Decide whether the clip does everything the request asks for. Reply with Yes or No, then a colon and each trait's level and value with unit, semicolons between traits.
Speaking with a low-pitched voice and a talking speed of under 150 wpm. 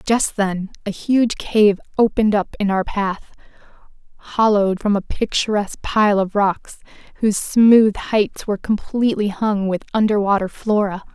No: high, 205 Hz; average, 140 wpm